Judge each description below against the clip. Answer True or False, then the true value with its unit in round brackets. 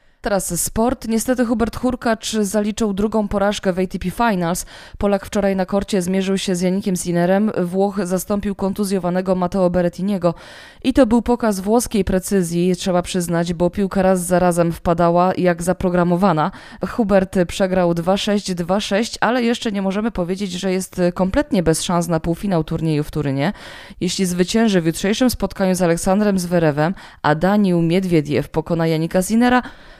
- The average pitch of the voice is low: False (190 Hz)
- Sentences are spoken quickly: False (150 wpm)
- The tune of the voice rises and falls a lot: False (2.7 semitones)